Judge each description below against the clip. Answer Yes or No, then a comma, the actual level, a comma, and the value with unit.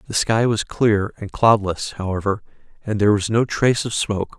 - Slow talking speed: No, average, 190 wpm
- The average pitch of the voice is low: Yes, low, 105 Hz